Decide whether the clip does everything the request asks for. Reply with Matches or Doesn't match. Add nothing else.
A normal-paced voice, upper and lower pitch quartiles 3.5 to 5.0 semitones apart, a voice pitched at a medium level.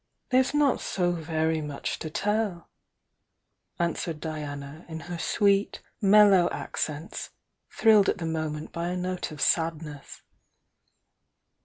Doesn't match